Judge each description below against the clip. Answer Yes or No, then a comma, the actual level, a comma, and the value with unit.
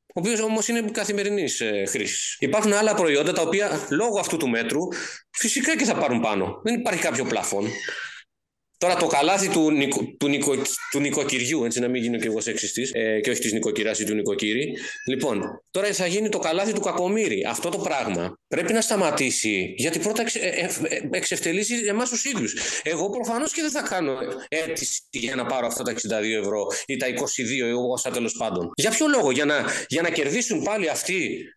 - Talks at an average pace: No, fast, 200 wpm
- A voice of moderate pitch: Yes, medium, 180 Hz